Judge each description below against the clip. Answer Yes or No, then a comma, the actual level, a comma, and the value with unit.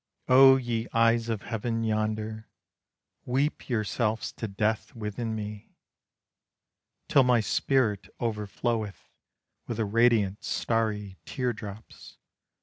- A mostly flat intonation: Yes, narrow, 2.0 semitones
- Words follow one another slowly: Yes, slow, 105 wpm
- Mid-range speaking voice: No, low, 110 Hz